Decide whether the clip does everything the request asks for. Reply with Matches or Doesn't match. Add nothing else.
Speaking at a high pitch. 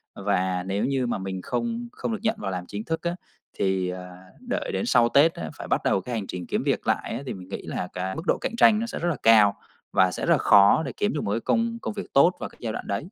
Doesn't match